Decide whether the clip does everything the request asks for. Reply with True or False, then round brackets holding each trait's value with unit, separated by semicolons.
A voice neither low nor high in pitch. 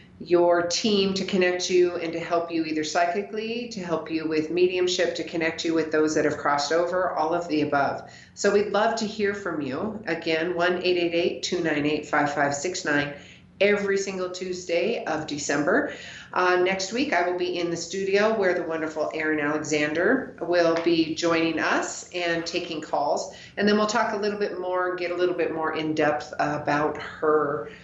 True (170 Hz)